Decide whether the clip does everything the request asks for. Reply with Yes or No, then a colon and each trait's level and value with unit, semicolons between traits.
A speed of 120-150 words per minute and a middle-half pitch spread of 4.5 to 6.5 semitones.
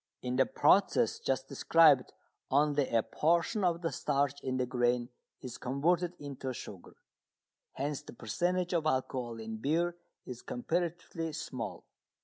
Yes: slow, 135 wpm; average, 4.8 semitones